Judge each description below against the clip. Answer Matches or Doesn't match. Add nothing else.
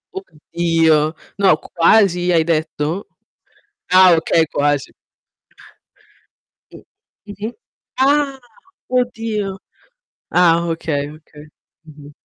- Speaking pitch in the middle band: Matches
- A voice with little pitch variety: Doesn't match